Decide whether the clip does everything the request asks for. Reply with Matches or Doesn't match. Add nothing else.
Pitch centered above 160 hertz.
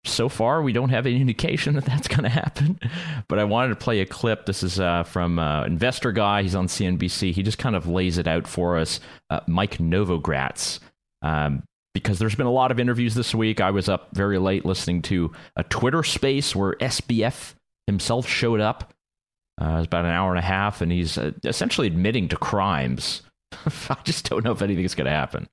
Doesn't match